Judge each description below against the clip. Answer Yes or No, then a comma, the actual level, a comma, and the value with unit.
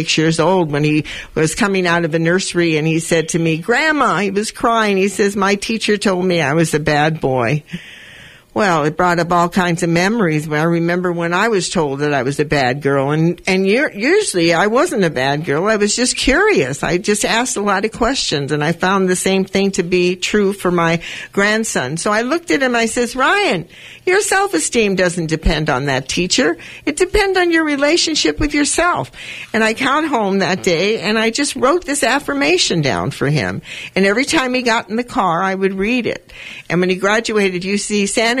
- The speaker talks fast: Yes, fast, 220 wpm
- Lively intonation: Yes, wide, 5.7 semitones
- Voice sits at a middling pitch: No, high, 195 Hz